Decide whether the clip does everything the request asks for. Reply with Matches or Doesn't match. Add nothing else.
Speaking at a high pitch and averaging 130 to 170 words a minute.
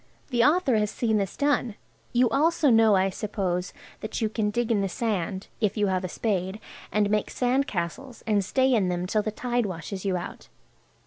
Doesn't match